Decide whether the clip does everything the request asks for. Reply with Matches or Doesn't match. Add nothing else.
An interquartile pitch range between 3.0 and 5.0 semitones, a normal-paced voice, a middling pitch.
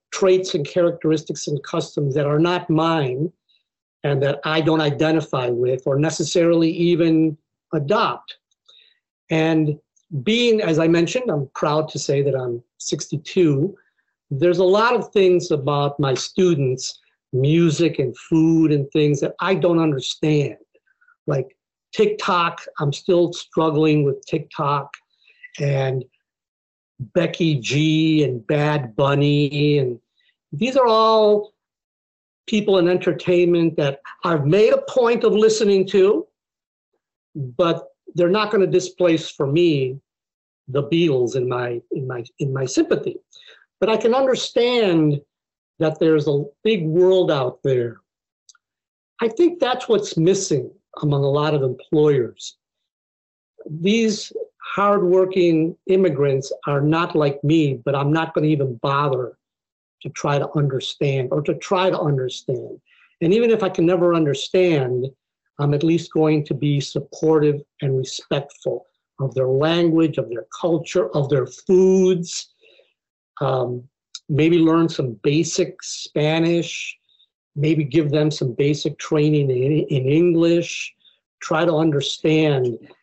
Doesn't match